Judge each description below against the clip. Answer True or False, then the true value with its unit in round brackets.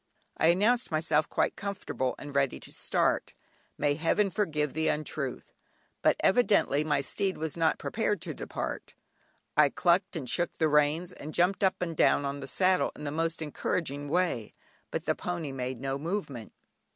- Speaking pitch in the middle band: True (155 Hz)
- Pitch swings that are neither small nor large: True (4.1 semitones)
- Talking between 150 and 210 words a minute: True (170 wpm)